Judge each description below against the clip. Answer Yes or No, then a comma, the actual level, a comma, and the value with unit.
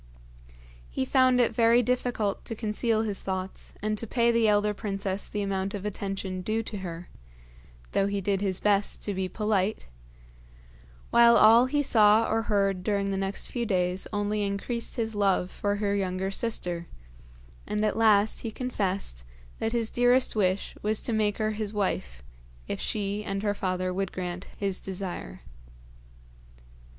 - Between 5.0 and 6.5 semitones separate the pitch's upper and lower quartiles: No, narrow, 2.4 semitones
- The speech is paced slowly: No, average, 160 wpm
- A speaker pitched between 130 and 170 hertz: No, high, 205 Hz